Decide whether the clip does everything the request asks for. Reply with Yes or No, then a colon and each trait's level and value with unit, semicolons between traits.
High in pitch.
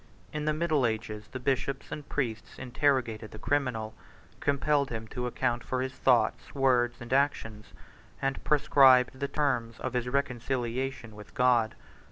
No: low, 125 Hz